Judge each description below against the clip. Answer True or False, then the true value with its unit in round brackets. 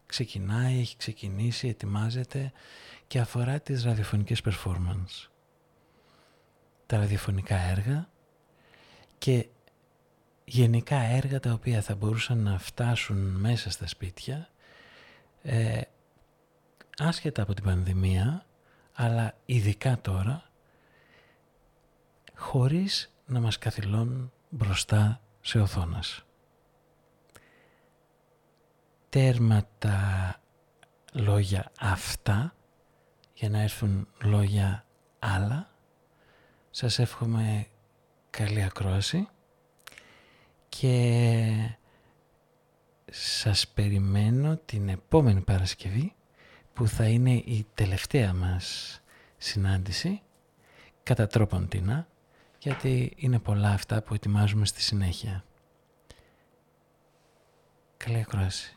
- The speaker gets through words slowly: True (80 wpm)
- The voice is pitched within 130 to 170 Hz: False (115 Hz)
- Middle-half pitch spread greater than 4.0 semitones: True (4.6 semitones)